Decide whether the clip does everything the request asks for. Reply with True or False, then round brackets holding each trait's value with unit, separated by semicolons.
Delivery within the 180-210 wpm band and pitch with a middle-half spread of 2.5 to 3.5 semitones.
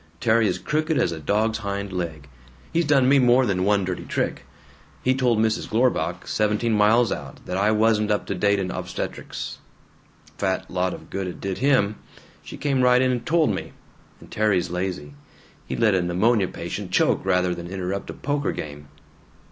False (185 wpm; 4.7 semitones)